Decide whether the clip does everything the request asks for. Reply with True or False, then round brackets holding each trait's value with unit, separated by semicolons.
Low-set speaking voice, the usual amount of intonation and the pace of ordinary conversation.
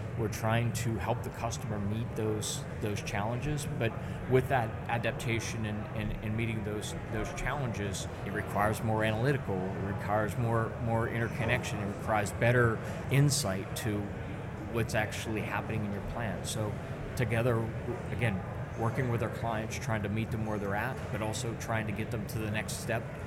False (115 Hz; 2.1 semitones; 170 wpm)